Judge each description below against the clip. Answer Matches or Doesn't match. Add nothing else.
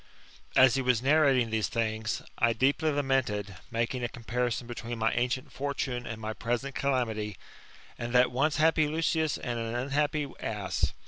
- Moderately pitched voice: Doesn't match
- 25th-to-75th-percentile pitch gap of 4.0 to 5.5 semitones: Doesn't match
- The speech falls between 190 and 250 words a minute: Doesn't match